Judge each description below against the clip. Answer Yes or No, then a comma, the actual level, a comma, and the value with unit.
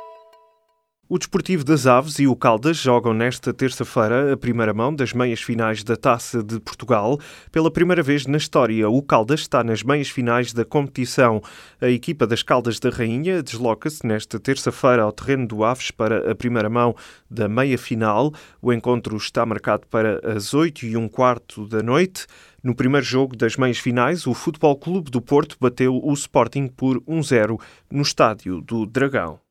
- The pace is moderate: Yes, average, 175 wpm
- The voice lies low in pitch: Yes, low, 125 Hz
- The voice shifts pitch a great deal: No, average, 3.7 semitones